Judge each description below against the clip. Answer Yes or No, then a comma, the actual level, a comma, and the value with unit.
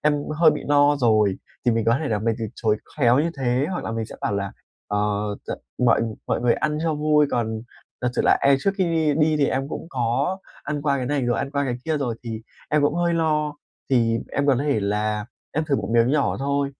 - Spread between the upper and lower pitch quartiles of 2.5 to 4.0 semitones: No, average, 4.5 semitones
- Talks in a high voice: No, medium, 140 Hz